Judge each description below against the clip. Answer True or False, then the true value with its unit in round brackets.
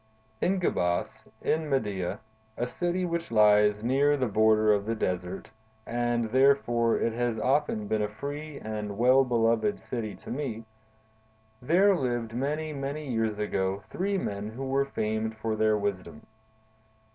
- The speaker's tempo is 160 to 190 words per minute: False (140 wpm)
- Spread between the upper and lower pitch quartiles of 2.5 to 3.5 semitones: False (4.2 semitones)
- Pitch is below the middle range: True (115 Hz)